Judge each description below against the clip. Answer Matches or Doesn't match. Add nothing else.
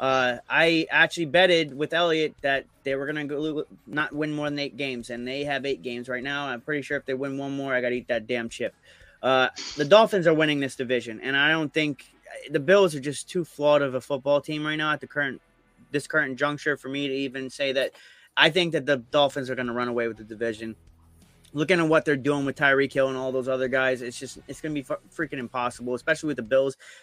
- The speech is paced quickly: Matches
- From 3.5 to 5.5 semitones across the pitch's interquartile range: Doesn't match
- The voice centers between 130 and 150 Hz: Matches